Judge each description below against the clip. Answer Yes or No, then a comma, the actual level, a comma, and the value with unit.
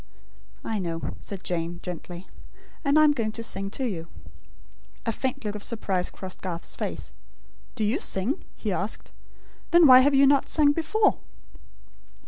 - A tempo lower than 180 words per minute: Yes, average, 160 wpm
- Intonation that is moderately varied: No, wide, 7.1 semitones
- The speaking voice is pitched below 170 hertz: No, high, 220 Hz